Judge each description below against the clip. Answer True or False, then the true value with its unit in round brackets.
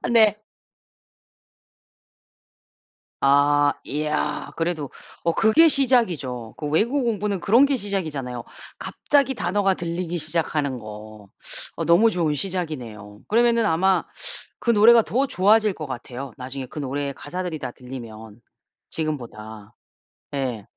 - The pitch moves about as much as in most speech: False (8.0 semitones)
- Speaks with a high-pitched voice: False (155 Hz)